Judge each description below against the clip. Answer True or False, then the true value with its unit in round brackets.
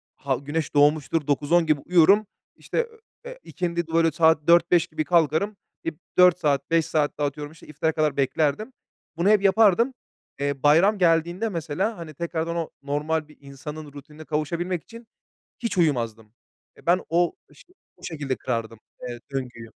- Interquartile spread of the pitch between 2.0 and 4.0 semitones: True (3.2 semitones)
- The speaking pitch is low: False (160 Hz)